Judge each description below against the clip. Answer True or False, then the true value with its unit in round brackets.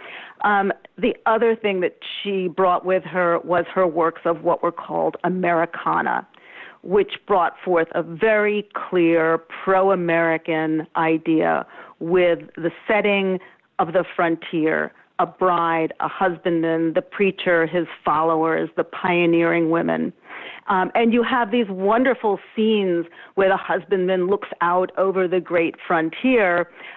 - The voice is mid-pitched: True (180 Hz)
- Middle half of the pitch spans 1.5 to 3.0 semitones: True (2.7 semitones)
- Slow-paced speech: True (130 wpm)